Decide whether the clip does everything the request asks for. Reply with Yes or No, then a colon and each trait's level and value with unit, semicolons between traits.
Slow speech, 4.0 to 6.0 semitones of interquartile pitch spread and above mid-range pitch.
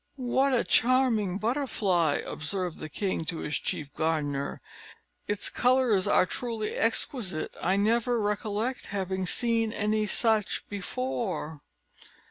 Yes: slow, 115 wpm; average, 4.7 semitones; high, 210 Hz